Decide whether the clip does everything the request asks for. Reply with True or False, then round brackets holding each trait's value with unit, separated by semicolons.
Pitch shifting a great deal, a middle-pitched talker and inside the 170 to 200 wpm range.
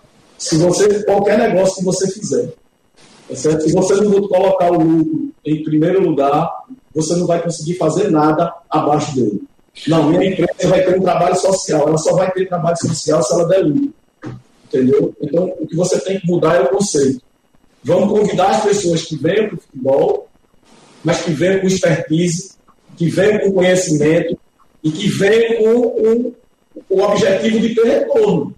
False (3.5 semitones; 180 Hz; 180 wpm)